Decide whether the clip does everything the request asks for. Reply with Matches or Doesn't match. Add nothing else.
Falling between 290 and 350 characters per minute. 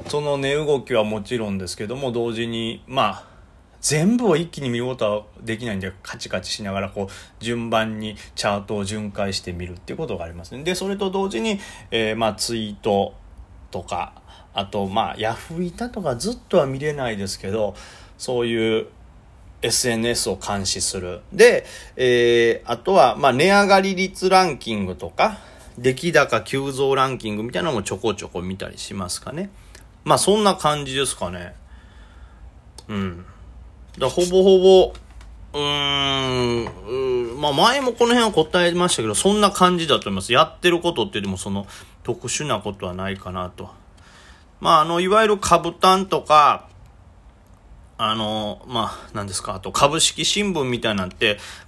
Matches